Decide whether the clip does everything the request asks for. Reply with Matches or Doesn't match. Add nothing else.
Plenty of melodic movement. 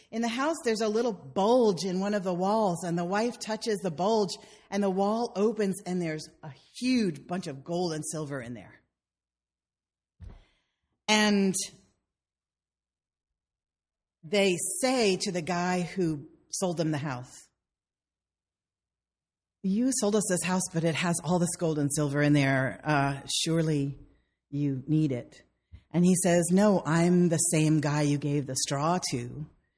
Matches